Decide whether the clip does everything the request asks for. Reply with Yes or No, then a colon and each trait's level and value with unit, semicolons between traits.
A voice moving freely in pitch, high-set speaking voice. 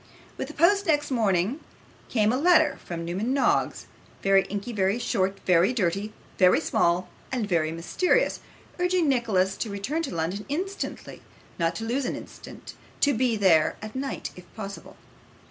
Yes: wide, 6.7 semitones; high, 215 Hz